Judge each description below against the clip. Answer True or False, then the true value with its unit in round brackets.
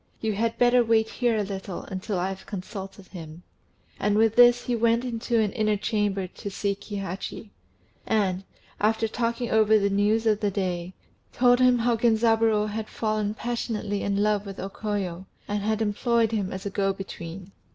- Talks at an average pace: True (180 wpm)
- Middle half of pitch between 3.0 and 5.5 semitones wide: False (2.4 semitones)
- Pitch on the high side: True (210 Hz)